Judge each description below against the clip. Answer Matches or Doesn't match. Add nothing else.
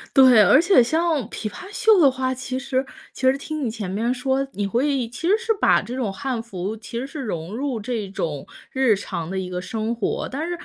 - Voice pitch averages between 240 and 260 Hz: Matches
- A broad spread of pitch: Doesn't match